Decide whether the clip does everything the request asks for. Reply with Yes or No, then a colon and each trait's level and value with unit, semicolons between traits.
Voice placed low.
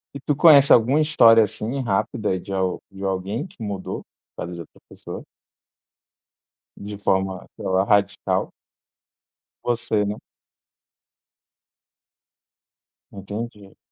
Yes: low, 105 Hz